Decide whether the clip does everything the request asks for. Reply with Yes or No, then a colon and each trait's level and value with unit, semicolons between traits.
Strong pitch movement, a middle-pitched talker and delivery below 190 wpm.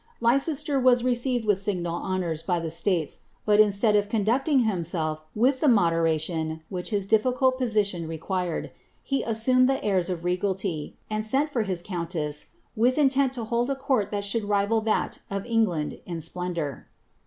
No: wide, 5.8 semitones; high, 205 Hz; average, 165 wpm